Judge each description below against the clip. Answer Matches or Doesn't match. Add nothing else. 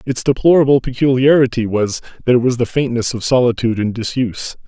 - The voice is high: Doesn't match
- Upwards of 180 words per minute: Doesn't match